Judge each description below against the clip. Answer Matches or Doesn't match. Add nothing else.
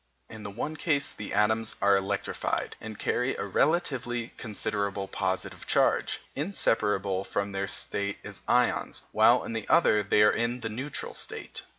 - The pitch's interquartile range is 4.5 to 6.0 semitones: Doesn't match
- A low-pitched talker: Matches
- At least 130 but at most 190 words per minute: Matches